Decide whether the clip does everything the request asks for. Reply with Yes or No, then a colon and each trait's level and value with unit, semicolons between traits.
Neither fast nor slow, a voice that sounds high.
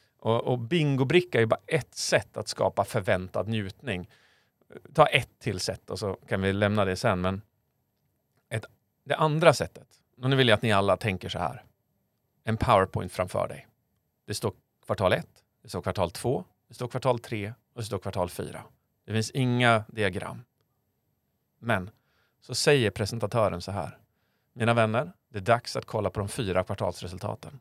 No: average, 170 wpm; low, 110 Hz